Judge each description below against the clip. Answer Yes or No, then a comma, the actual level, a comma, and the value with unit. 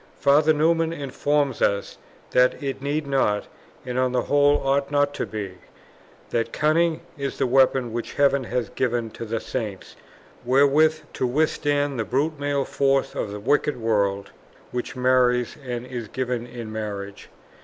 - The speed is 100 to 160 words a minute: Yes, average, 155 wpm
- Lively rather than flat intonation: No, average, 3.4 semitones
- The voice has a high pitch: No, low, 130 Hz